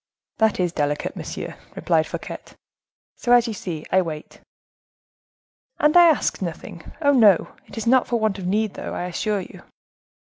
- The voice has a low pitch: No, high, 205 Hz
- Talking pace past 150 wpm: Yes, average, 165 wpm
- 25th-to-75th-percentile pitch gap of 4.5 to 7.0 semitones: Yes, average, 5.2 semitones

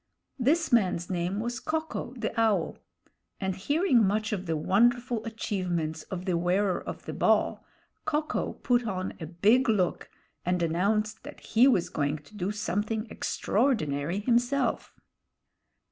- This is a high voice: Yes, high, 210 Hz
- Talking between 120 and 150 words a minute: Yes, average, 145 wpm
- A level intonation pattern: No, average, 5.0 semitones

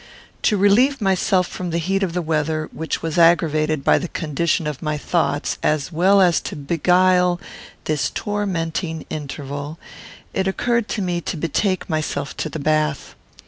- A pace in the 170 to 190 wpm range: No, average, 160 wpm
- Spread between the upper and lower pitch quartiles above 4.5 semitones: No, average, 3.3 semitones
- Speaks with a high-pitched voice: No, medium, 165 Hz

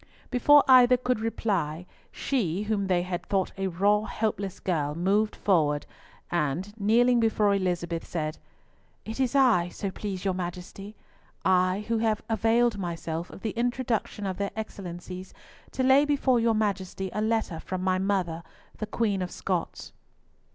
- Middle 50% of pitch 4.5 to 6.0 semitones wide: No, average, 3.8 semitones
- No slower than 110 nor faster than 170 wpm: Yes, average, 150 wpm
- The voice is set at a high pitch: Yes, high, 200 Hz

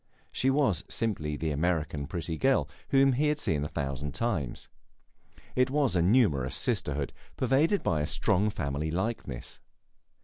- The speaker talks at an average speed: Yes, average, 145 wpm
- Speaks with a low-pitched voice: Yes, very low, 90 Hz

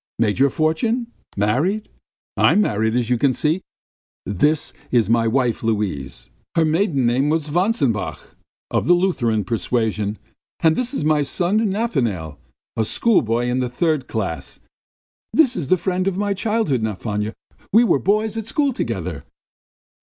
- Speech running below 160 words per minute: Yes, average, 150 wpm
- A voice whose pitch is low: No, medium, 145 Hz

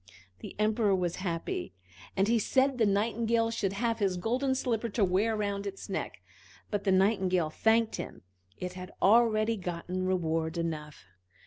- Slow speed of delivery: No, average, 155 wpm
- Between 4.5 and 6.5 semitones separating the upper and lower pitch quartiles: No, average, 3.7 semitones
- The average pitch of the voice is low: No, high, 200 Hz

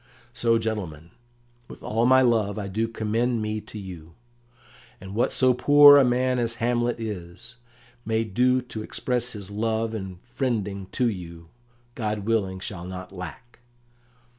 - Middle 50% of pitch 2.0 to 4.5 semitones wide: Yes, average, 3.9 semitones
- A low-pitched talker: Yes, low, 110 Hz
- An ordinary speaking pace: Yes, average, 150 wpm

